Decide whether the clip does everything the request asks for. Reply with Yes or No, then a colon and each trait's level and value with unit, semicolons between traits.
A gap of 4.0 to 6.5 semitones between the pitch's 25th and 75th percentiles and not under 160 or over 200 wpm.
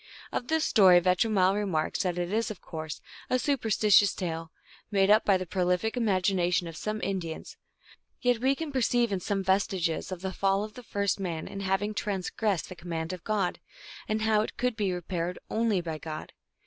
No: average, 3.3 semitones; average, 190 wpm